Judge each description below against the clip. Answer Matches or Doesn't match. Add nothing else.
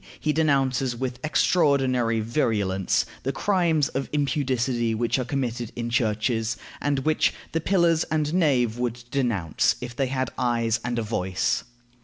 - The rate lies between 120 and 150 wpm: Matches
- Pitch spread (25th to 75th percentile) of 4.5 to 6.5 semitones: Doesn't match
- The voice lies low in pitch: Matches